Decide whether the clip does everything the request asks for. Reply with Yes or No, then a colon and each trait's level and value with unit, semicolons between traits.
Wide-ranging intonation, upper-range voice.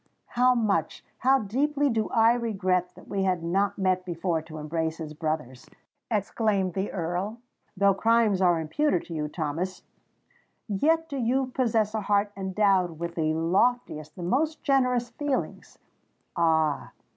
Yes: wide, 5.8 semitones; high, 195 Hz